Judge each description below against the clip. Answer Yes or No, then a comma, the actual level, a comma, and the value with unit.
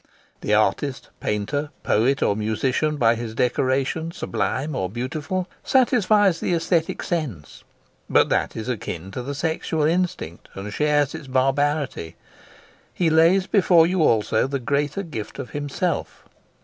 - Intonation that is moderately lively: No, wide, 5.8 semitones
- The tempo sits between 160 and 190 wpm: No, slow, 135 wpm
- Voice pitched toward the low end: No, medium, 145 Hz